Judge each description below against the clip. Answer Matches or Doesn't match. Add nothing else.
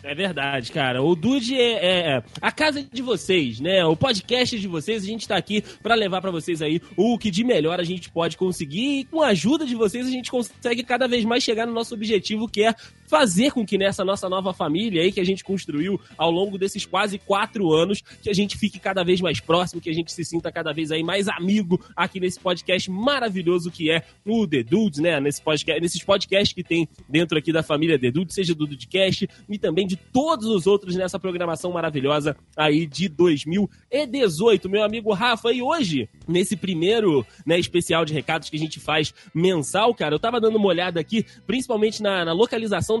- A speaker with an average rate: Doesn't match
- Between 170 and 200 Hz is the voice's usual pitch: Matches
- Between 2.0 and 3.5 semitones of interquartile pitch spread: Doesn't match